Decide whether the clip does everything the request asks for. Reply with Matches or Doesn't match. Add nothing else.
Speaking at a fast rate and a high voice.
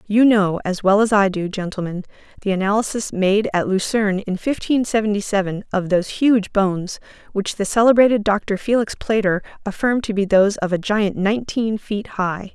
Doesn't match